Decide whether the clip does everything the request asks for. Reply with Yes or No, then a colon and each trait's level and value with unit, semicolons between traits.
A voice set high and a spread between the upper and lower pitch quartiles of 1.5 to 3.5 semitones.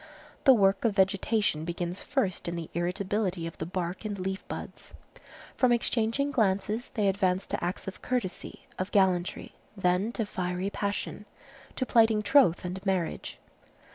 Yes: high, 195 Hz; average, 3.2 semitones